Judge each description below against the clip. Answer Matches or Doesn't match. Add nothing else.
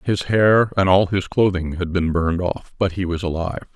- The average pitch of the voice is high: Doesn't match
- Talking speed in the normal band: Doesn't match